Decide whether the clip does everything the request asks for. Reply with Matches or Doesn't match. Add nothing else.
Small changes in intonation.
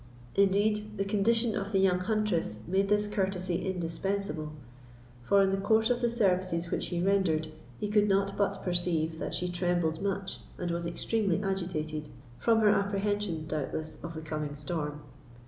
Doesn't match